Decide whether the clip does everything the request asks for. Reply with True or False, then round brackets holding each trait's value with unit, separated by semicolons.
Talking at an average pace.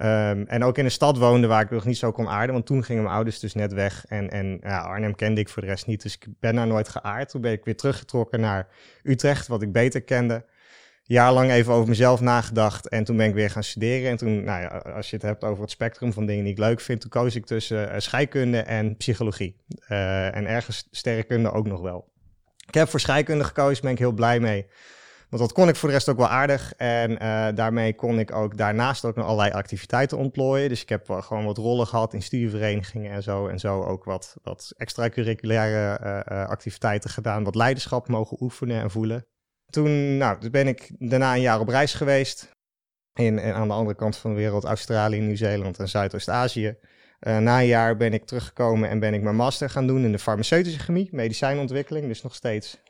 False (230 wpm)